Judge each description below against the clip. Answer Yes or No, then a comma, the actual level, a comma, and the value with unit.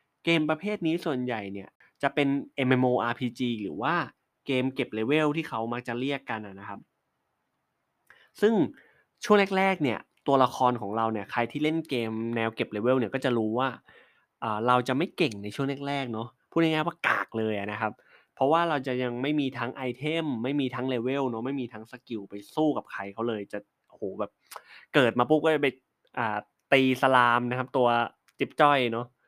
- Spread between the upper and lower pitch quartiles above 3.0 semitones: Yes, average, 3.5 semitones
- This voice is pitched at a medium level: No, low, 125 Hz